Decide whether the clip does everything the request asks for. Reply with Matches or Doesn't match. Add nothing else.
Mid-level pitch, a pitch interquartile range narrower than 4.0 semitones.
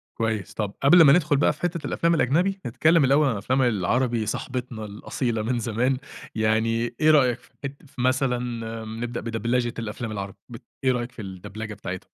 Doesn't match